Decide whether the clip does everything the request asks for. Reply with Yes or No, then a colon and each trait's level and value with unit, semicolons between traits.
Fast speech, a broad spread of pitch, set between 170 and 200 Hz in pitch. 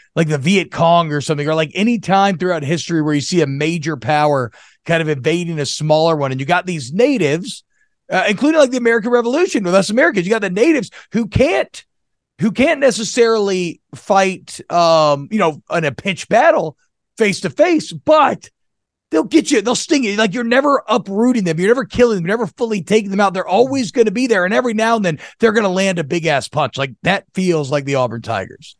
Yes: fast, 215 wpm; wide, 6.4 semitones; high, 190 Hz